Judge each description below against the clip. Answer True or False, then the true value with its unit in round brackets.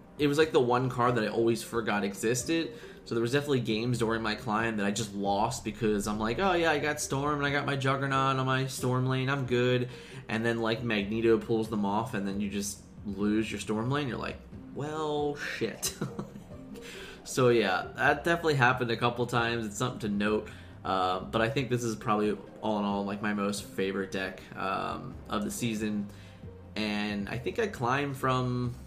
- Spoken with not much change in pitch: False (4.0 semitones)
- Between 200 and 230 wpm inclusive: True (205 wpm)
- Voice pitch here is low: True (115 Hz)